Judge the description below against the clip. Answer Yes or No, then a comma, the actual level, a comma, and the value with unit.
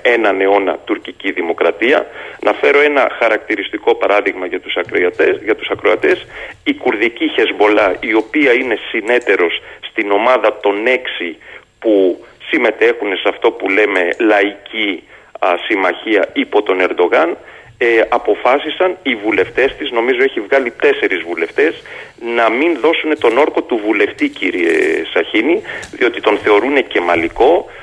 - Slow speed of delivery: No, average, 130 wpm